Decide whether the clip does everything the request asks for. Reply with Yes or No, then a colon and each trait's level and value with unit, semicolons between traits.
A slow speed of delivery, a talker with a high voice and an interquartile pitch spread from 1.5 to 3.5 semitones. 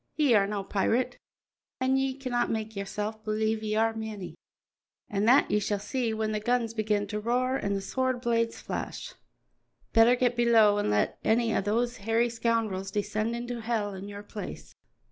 No: average, 180 wpm; high, 220 Hz; narrow, 2.5 semitones